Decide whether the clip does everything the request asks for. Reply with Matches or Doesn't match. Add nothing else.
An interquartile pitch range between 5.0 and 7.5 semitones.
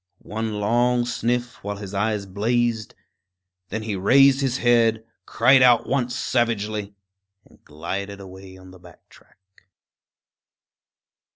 Doesn't match